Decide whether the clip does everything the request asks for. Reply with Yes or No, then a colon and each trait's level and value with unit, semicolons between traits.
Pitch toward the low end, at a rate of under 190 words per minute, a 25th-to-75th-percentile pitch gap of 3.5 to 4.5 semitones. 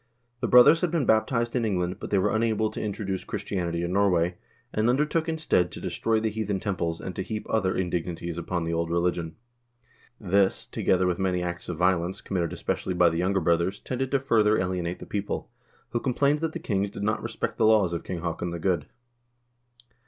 No: very low, 95 Hz; average, 200 wpm; average, 4.1 semitones